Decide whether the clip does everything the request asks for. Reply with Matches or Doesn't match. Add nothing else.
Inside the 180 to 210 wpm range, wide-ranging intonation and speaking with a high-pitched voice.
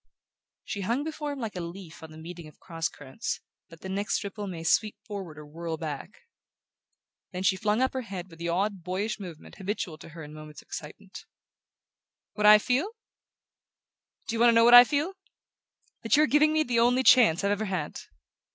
Matches